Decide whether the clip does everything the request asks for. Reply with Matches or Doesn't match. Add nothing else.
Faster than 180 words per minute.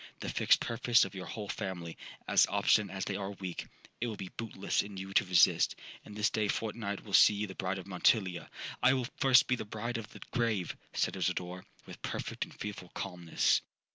Matches